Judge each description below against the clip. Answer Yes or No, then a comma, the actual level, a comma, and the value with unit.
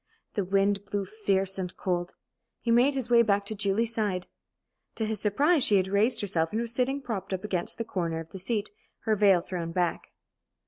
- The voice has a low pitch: No, high, 200 Hz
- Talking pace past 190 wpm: Yes, average, 200 wpm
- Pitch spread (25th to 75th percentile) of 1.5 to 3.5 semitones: Yes, average, 3.2 semitones